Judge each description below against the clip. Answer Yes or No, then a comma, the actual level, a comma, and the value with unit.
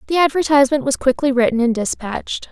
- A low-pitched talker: No, very high, 265 Hz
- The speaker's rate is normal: Yes, average, 165 wpm